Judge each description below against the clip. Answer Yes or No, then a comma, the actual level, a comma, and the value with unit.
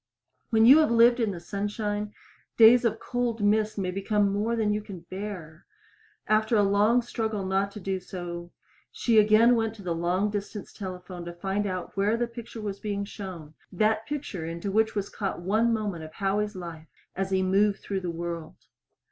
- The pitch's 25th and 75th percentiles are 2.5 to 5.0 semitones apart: Yes, average, 2.8 semitones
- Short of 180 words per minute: No, average, 190 wpm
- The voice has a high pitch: Yes, high, 205 Hz